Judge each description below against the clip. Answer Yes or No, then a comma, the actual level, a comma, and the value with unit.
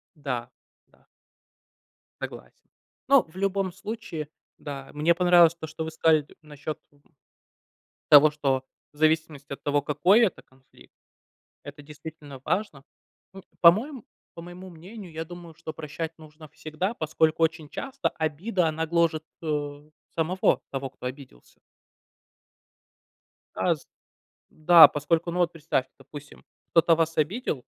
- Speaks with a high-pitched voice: No, medium, 160 Hz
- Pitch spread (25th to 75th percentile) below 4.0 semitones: Yes, average, 2.8 semitones